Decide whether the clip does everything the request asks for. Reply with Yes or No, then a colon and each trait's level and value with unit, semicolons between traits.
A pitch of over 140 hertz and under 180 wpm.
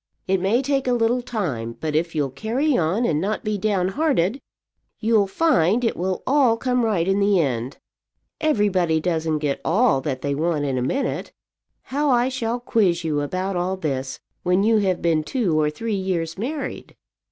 No: high, 190 Hz; average, 185 wpm